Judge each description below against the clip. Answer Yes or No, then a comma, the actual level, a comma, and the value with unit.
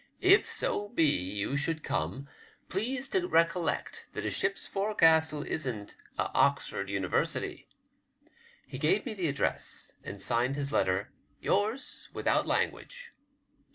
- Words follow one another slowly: Yes, slow, 130 wpm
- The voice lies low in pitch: No, medium, 155 Hz